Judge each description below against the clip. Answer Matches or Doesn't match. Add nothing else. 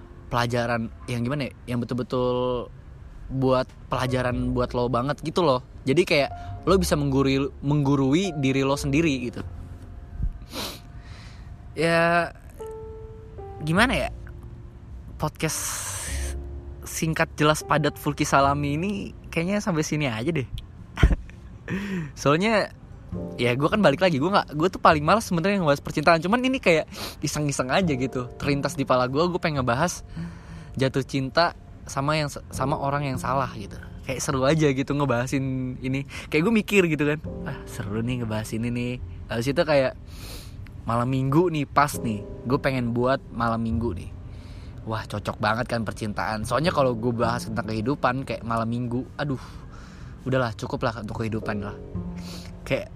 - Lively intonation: Doesn't match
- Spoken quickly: Matches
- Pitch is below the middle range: Matches